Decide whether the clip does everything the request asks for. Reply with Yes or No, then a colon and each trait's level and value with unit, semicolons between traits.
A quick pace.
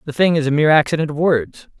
Yes: fast, 265 wpm